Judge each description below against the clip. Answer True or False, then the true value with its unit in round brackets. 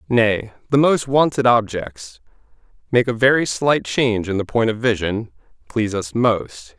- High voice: False (110 Hz)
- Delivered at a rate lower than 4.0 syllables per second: True (2.6 syllables/s)